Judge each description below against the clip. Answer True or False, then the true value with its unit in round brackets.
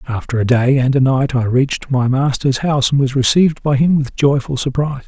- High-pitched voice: False (135 Hz)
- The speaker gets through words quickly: True (225 wpm)